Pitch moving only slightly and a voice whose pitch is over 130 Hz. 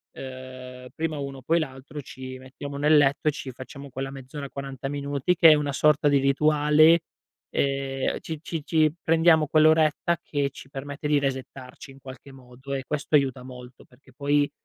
Yes: narrow, 2.2 semitones; medium, 140 Hz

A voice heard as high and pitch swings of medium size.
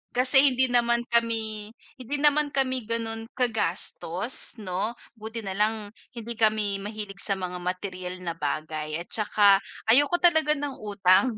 Yes: high, 220 Hz; average, 4.2 semitones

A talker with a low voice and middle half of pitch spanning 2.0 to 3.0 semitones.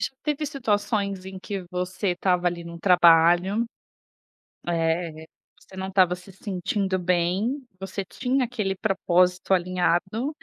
No: medium, 185 Hz; narrow, 2.5 semitones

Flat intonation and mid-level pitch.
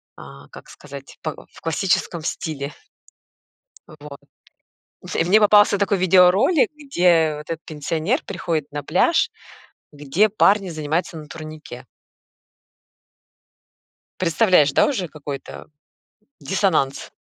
No: average, 4.6 semitones; medium, 165 Hz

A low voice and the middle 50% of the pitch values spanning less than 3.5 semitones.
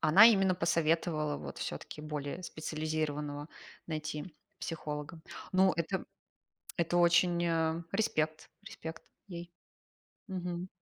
No: medium, 165 Hz; narrow, 2.5 semitones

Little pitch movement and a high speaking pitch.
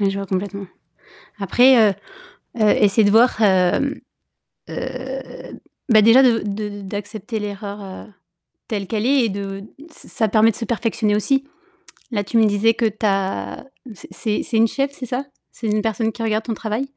Yes: narrow, 2.2 semitones; high, 215 Hz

